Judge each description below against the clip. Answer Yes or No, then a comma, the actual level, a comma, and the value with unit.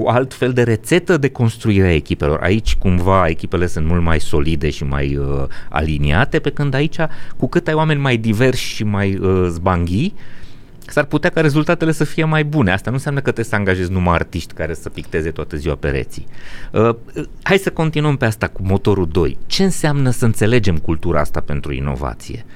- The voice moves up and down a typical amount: No, wide, 8.8 semitones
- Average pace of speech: No, fast, 195 wpm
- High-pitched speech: No, low, 105 Hz